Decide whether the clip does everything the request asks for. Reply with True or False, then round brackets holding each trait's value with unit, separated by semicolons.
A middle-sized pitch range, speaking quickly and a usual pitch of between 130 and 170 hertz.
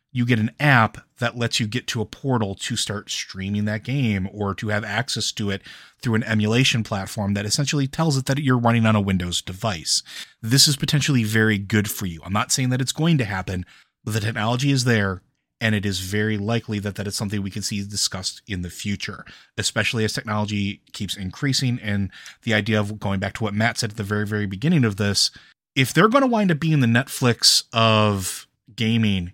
False (3.4 semitones; 215 wpm; 110 Hz)